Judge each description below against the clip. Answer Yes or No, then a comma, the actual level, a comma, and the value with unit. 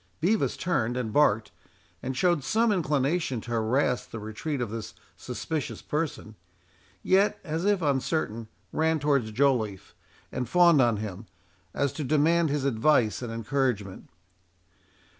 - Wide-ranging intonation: Yes, wide, 5.8 semitones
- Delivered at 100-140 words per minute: Yes, slow, 135 wpm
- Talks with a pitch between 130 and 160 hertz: Yes, low, 135 Hz